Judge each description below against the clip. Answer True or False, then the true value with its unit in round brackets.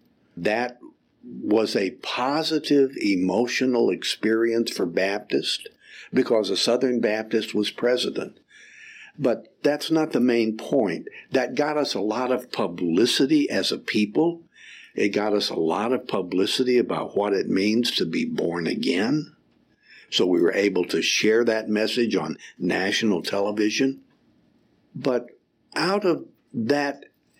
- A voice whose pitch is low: True (120 Hz)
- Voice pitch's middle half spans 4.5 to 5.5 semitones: True (4.8 semitones)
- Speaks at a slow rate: True (130 wpm)